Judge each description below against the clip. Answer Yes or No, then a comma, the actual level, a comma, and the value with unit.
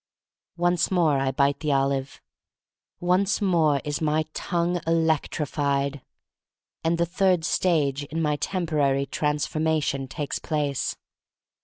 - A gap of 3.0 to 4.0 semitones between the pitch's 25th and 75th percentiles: Yes, average, 3.3 semitones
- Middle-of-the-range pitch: Yes, medium, 155 Hz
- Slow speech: Yes, slow, 120 wpm